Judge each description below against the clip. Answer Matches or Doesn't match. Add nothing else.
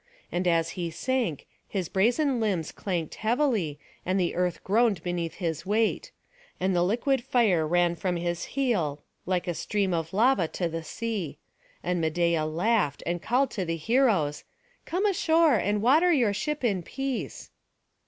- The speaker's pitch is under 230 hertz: Matches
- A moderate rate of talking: Matches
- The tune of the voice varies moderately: Doesn't match